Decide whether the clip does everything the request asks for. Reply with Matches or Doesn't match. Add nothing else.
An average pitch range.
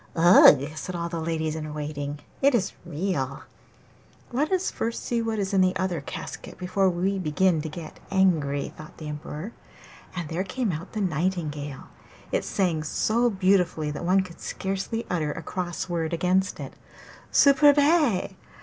Matches